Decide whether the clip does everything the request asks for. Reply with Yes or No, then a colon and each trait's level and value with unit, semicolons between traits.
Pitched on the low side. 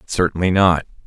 Yes: very low, 90 Hz